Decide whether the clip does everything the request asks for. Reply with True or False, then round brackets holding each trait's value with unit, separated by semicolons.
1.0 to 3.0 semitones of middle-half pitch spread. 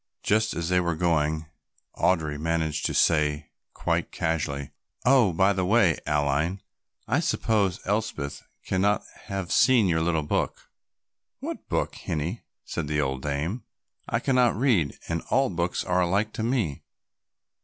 False (5.2 semitones)